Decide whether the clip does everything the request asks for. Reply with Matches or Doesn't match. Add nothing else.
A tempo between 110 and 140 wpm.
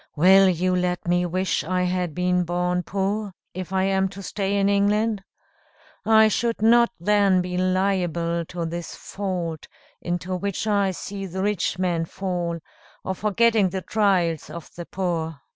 Doesn't match